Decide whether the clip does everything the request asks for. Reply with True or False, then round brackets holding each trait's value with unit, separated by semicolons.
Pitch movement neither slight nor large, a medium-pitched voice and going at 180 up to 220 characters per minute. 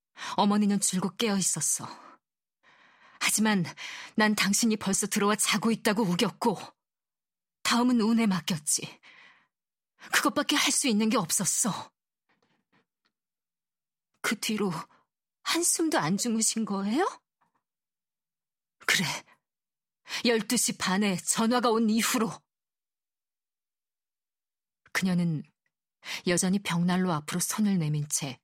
False (4.0 semitones; 210 Hz; 200 characters per minute)